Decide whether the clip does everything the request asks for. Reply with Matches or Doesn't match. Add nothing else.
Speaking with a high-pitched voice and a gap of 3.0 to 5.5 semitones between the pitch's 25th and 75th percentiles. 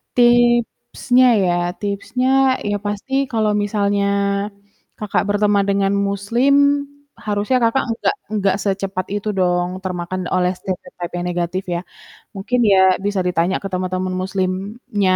Doesn't match